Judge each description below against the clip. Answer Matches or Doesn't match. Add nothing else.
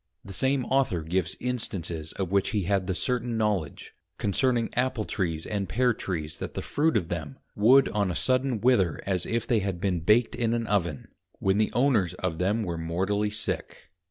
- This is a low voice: Matches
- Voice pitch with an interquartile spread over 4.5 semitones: Matches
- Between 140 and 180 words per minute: Doesn't match